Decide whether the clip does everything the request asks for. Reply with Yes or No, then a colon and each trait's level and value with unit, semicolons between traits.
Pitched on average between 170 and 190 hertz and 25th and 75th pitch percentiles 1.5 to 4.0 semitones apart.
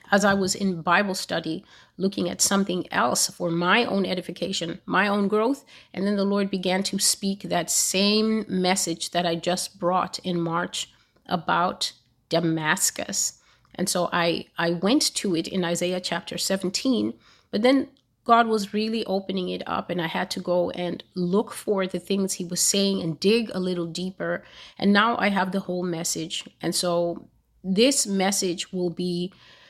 Yes: medium, 185 Hz; narrow, 2.4 semitones